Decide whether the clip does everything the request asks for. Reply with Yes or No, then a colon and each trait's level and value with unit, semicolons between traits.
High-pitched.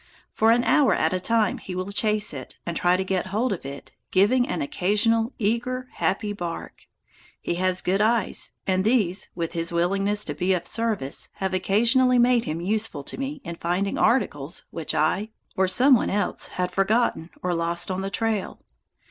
Yes: high, 195 Hz